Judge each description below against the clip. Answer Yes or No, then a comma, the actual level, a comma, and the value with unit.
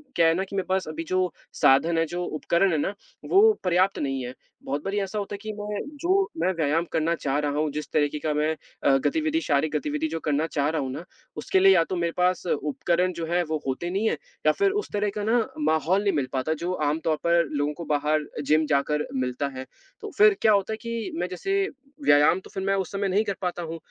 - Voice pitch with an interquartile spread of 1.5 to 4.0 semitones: No, average, 4.6 semitones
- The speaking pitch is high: No, medium, 170 Hz